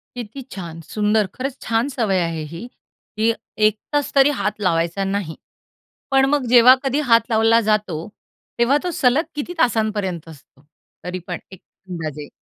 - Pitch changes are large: Yes, wide, 6.0 semitones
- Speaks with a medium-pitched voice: No, high, 215 Hz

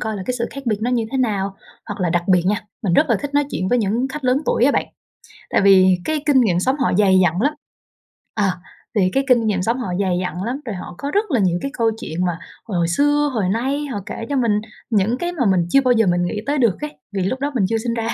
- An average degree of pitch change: No, wide, 5.8 semitones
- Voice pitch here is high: Yes, high, 225 Hz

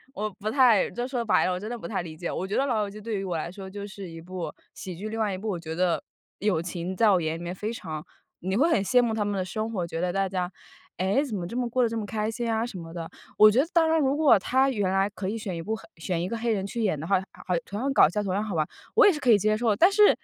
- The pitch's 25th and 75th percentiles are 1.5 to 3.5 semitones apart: No, average, 3.9 semitones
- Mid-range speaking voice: No, high, 205 Hz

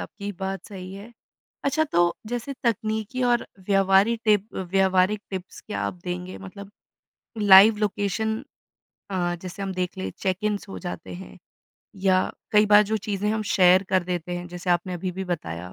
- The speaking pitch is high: Yes, high, 195 Hz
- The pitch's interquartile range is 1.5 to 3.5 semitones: Yes, narrow, 2.5 semitones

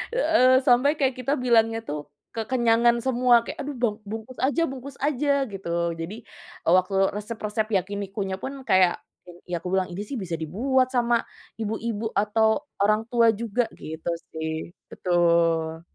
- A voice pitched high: Yes, high, 220 Hz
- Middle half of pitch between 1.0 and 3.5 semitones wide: No, average, 5.1 semitones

